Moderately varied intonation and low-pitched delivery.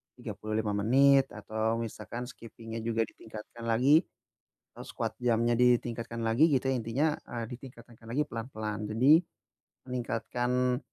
No: narrow, 2.1 semitones; low, 115 Hz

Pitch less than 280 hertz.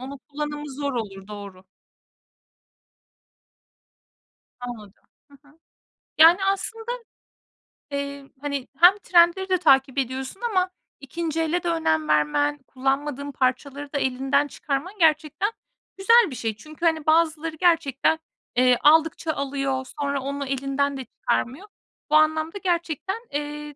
No: very high, 290 Hz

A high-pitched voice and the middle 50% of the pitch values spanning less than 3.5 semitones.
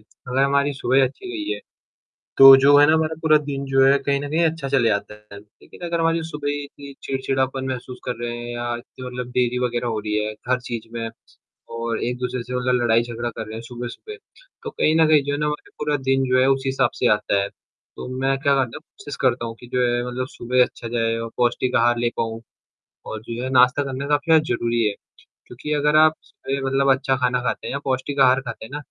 No: low, 130 Hz; average, 2.9 semitones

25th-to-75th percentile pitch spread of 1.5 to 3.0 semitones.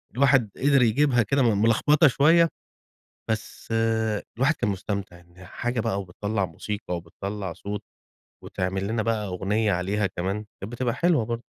No: average, 3.7 semitones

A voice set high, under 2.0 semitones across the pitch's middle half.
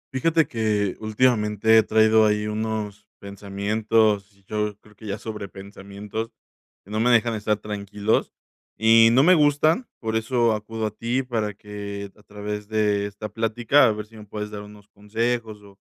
No: low, 105 Hz; narrow, 1.5 semitones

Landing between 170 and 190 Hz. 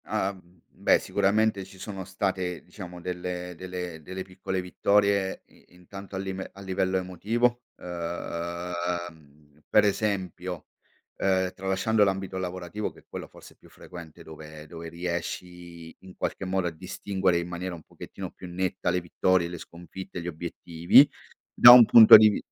No: very low, 90 Hz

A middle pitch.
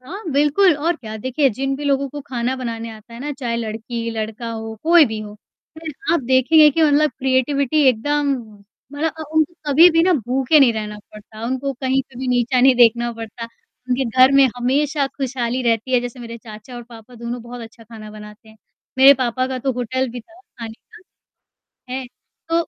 No: very high, 255 Hz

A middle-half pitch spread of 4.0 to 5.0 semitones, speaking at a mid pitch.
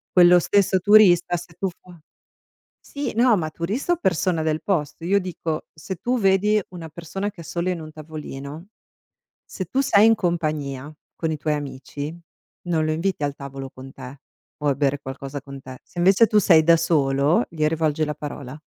Yes: average, 4.3 semitones; medium, 165 Hz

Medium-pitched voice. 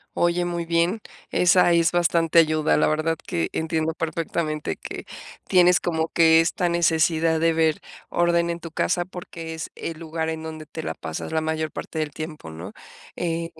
Yes: medium, 165 Hz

